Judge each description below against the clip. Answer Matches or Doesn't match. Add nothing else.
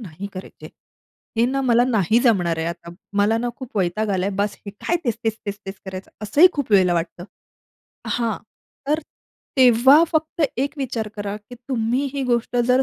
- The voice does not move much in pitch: Doesn't match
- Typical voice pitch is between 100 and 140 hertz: Doesn't match